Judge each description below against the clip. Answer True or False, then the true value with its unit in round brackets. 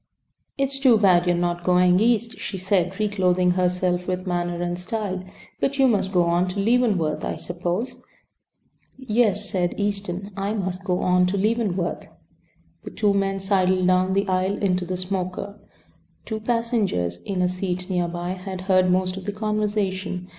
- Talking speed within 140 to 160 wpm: False (170 wpm)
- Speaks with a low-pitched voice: False (185 Hz)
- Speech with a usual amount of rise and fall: False (2.3 semitones)